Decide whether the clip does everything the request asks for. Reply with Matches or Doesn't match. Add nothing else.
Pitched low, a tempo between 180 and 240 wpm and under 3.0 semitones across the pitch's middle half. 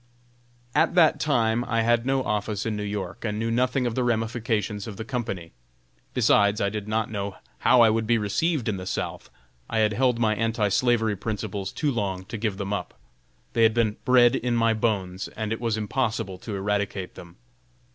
Matches